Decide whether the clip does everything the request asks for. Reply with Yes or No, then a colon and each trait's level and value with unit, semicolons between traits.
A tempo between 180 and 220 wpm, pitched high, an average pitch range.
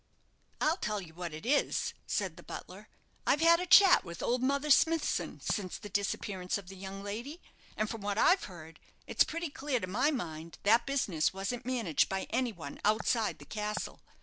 No: average, 190 wpm; high, 210 Hz; wide, 6.5 semitones